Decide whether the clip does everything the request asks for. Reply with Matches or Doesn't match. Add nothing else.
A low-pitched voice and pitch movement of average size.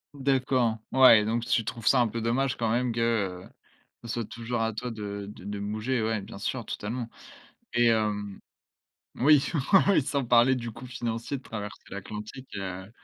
Matches